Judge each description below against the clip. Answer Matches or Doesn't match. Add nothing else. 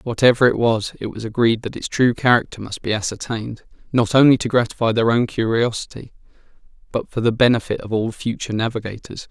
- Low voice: Matches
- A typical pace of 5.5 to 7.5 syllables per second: Matches